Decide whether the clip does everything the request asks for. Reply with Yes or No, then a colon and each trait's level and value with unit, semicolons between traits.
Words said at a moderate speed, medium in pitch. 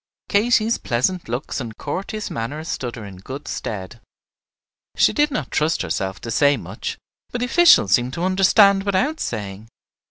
Yes: average, 160 wpm; medium, 145 Hz